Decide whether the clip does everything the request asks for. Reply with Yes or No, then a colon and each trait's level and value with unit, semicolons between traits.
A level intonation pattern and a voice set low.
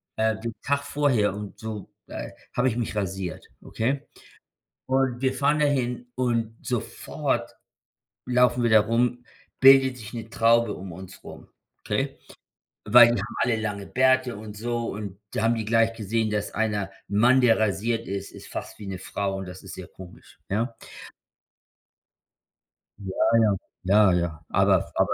No: average, 3.2 semitones; low, 115 Hz